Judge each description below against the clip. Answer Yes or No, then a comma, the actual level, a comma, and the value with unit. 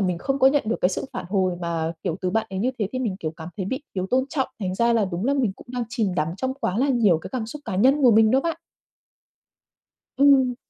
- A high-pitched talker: Yes, high, 225 Hz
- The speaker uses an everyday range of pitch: No, wide, 6.0 semitones